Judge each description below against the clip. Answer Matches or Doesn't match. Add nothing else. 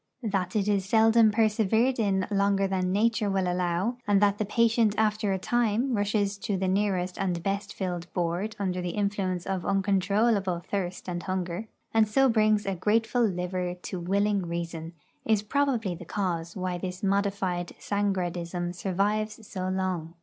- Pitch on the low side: Doesn't match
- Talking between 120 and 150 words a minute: Doesn't match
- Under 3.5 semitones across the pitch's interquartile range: Matches